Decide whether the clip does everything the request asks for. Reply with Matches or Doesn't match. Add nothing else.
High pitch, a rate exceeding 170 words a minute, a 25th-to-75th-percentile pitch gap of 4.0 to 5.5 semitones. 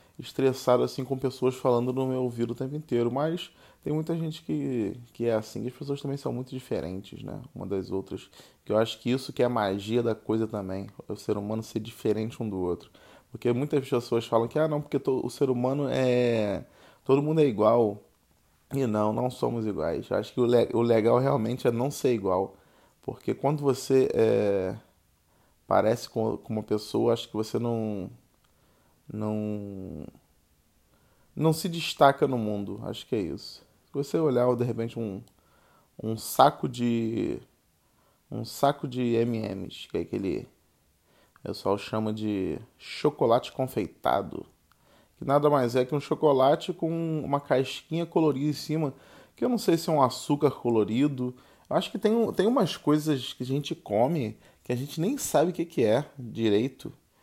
Doesn't match